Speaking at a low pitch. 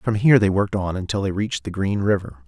Yes: low, 100 Hz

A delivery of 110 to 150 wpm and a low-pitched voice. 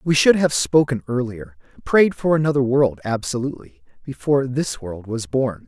No: average, 160 wpm; low, 130 Hz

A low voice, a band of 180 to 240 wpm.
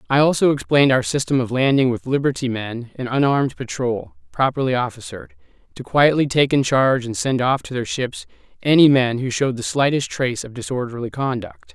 Yes: low, 130 Hz; average, 185 wpm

